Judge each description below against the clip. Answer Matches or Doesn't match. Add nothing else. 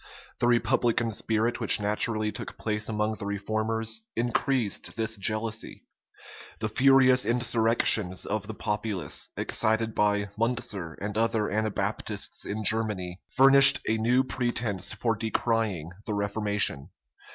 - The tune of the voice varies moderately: Doesn't match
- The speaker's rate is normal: Doesn't match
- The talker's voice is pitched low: Matches